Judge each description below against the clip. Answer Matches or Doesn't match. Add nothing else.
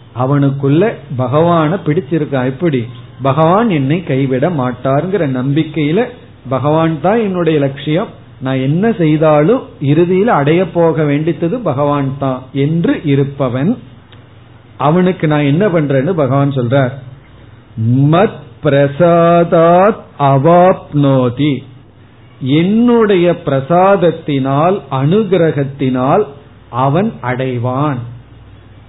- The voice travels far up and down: Doesn't match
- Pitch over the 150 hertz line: Doesn't match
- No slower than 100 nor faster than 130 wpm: Doesn't match